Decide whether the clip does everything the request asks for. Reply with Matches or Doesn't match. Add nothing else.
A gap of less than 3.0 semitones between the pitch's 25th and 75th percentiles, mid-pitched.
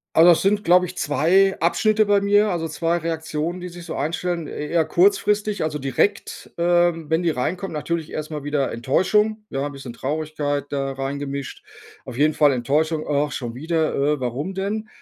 Doesn't match